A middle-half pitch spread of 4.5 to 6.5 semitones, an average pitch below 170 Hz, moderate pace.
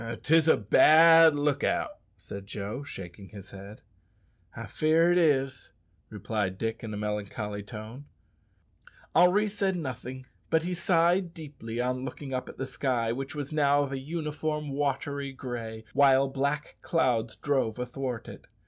Yes: average, 5.2 semitones; low, 135 Hz; average, 150 wpm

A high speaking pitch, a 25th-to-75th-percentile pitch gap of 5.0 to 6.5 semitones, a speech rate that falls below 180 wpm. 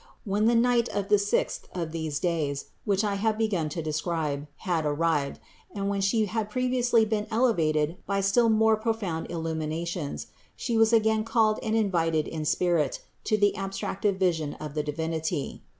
Yes: high, 195 Hz; average, 5.3 semitones; average, 165 wpm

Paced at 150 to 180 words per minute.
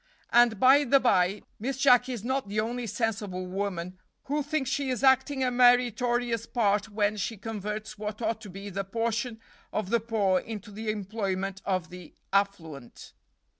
Yes: average, 170 wpm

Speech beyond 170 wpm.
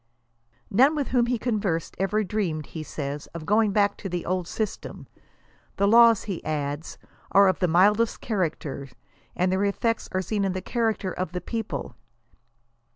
No: average, 165 wpm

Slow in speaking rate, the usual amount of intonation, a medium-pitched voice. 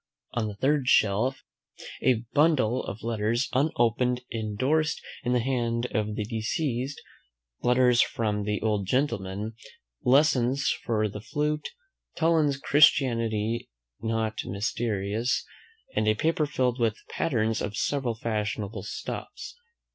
No: slow, 115 wpm; average, 3.6 semitones; low, 115 Hz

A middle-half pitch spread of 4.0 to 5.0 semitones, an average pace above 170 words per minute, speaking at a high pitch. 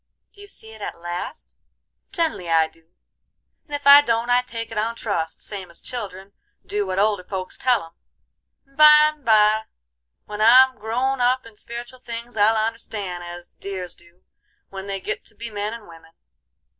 Yes: average, 4.4 semitones; average, 180 wpm; high, 220 Hz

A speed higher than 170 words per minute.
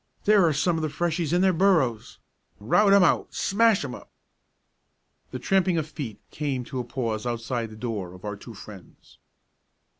Yes: average, 180 wpm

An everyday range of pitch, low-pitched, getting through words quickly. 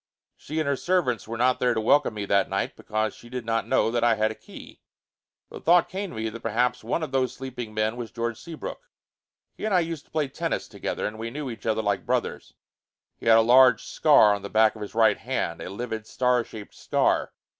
Yes: average, 3.2 semitones; low, 115 Hz; fast, 235 wpm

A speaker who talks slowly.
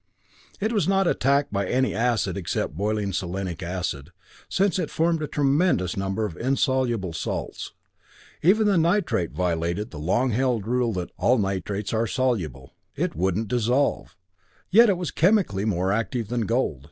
No: average, 155 wpm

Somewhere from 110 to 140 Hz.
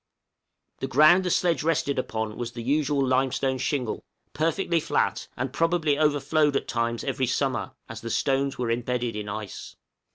Yes: low, 135 Hz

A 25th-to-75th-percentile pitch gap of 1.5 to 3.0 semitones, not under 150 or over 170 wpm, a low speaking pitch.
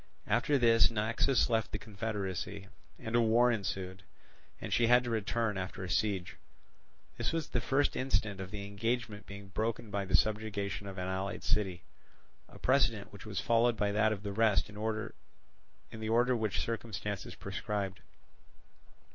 Yes: narrow, 2.5 semitones; average, 160 wpm; low, 110 Hz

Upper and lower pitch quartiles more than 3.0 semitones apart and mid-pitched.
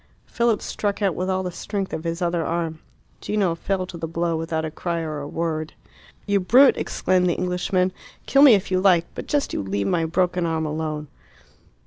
No: average, 2.7 semitones; medium, 175 Hz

